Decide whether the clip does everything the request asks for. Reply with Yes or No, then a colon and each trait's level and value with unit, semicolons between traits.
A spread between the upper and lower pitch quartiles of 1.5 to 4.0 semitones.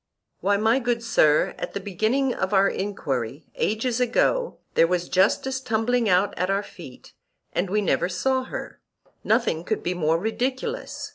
No: average, 5.3 semitones